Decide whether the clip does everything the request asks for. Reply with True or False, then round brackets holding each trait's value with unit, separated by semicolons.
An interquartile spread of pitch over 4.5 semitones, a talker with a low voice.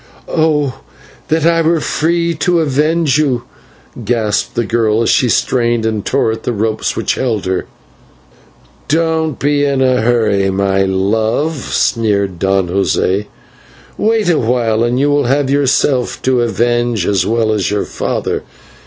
True (5.1 semitones; 120 Hz)